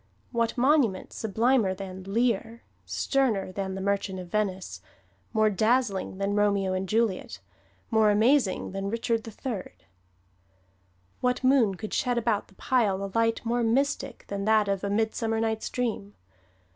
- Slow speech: No, average, 145 wpm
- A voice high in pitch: Yes, high, 215 Hz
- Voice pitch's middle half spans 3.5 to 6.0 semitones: No, average, 3.1 semitones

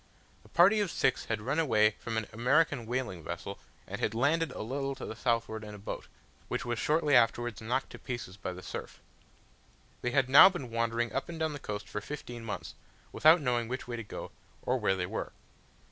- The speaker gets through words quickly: Yes, fast, 210 wpm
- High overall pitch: No, low, 120 Hz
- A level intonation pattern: No, average, 4.0 semitones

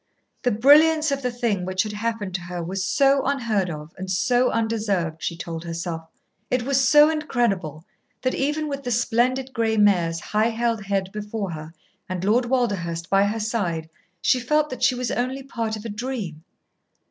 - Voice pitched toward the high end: Yes, high, 220 Hz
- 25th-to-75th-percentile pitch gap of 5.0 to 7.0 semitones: Yes, wide, 5.4 semitones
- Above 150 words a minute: Yes, average, 180 wpm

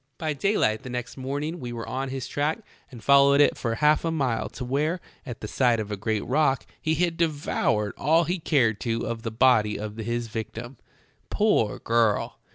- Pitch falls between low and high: No, low, 130 Hz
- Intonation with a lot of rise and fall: No, average, 4.7 semitones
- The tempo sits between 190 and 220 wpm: Yes, average, 195 wpm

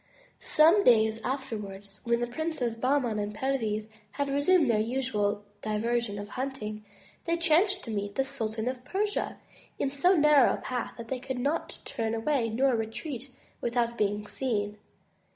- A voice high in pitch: Yes, high, 240 Hz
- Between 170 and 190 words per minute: No, average, 160 wpm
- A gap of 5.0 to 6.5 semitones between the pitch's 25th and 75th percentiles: No, average, 4.2 semitones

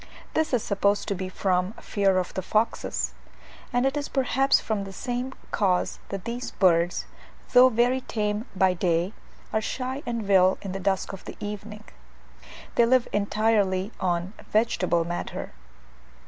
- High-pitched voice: Yes, high, 205 Hz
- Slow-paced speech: No, average, 155 wpm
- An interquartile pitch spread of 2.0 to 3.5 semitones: No, average, 4.2 semitones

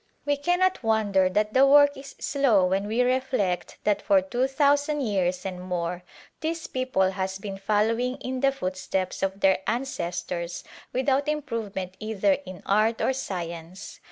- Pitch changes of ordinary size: No, wide, 6.1 semitones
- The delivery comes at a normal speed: Yes, average, 155 wpm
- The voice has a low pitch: No, high, 215 Hz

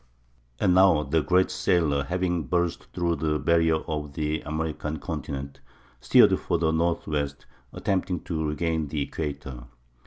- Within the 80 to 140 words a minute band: Yes, slow, 135 wpm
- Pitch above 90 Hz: No, very low, 80 Hz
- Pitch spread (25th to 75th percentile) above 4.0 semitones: No, narrow, 2.5 semitones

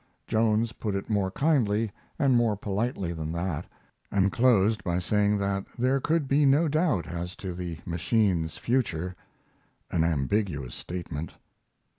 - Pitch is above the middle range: No, low, 100 Hz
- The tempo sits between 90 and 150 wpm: Yes, average, 140 wpm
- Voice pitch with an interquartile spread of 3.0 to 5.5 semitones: Yes, average, 5.1 semitones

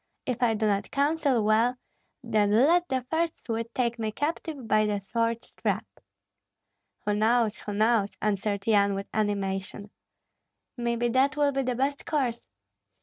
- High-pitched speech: Yes, high, 230 Hz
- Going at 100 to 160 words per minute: Yes, average, 150 wpm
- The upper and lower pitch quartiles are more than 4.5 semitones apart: No, average, 3.8 semitones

